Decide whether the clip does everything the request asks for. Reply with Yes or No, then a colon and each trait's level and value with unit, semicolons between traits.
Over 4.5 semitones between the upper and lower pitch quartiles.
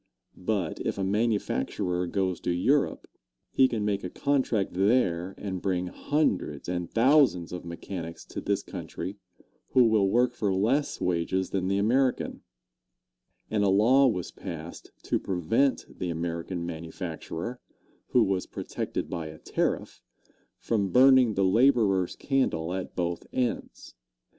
Yes: average, 5.2 semitones